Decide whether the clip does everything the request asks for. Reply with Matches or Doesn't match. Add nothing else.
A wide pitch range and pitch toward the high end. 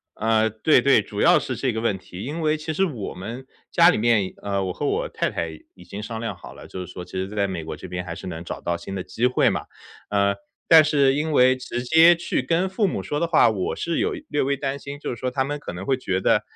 Doesn't match